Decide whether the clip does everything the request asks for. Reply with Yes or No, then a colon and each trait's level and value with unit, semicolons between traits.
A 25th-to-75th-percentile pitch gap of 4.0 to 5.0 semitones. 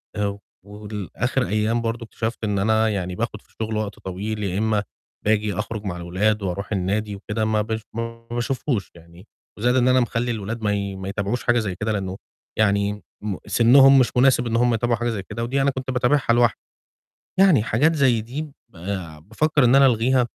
No: average, 3.0 semitones